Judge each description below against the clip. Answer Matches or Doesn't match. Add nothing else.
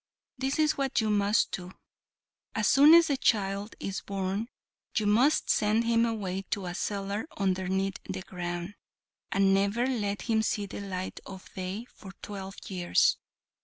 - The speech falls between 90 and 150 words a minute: Doesn't match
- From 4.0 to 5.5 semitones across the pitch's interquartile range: Doesn't match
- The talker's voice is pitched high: Matches